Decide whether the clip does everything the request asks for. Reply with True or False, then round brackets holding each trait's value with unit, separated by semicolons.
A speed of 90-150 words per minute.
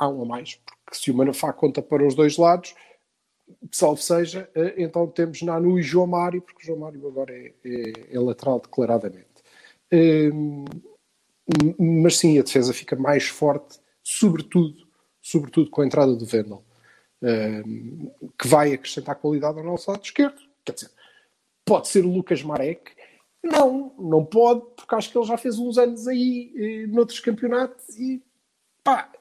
False (160 wpm)